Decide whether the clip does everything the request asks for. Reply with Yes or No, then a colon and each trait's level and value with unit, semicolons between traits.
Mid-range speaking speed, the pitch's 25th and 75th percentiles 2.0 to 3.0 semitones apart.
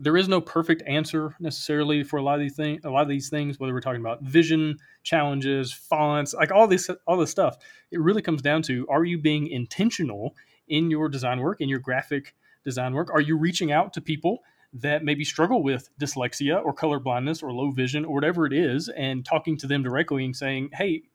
No: fast, 220 wpm; average, 2.7 semitones